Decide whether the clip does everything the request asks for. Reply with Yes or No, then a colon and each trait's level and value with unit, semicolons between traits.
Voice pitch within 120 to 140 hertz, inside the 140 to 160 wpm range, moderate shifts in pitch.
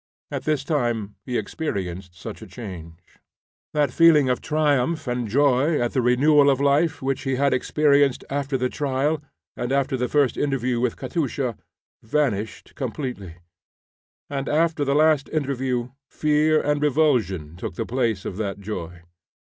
Yes: low, 135 Hz; average, 150 wpm; average, 3.7 semitones